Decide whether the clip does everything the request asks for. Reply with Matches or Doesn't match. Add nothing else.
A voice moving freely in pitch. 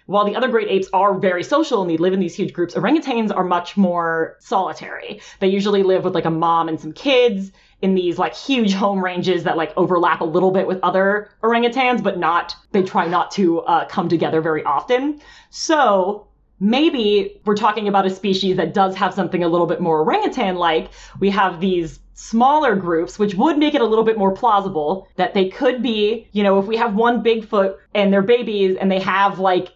Doesn't match